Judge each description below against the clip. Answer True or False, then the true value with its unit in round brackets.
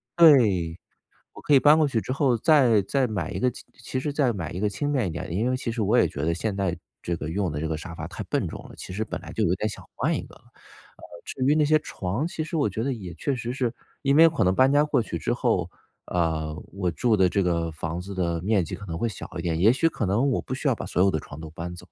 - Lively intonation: True (7.1 semitones)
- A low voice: True (105 Hz)